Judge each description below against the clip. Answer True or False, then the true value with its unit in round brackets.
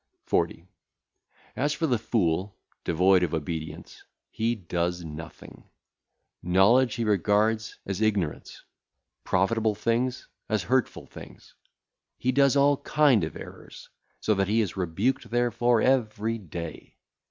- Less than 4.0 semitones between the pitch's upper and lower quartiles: False (5.2 semitones)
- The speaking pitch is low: True (110 Hz)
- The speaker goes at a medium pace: False (120 wpm)